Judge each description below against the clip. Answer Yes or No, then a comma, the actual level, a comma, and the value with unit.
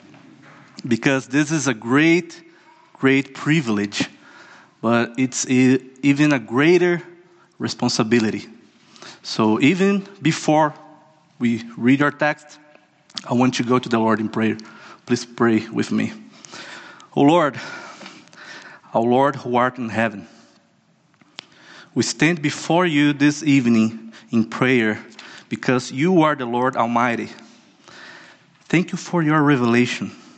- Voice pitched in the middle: No, low, 130 Hz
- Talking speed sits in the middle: No, slow, 125 wpm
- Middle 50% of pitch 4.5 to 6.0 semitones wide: Yes, average, 4.8 semitones